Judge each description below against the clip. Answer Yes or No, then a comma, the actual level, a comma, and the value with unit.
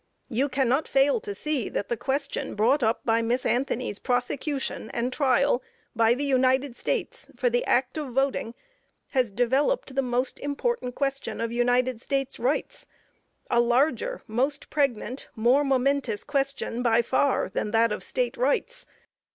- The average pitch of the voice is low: No, very high, 255 Hz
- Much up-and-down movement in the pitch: No, average, 2.7 semitones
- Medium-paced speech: Yes, average, 150 wpm